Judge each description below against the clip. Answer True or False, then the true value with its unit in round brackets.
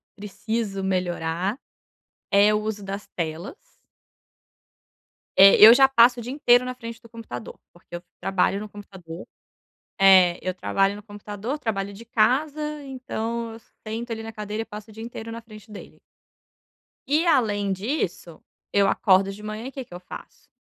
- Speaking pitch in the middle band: False (210 Hz)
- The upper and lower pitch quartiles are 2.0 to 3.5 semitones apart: True (3.0 semitones)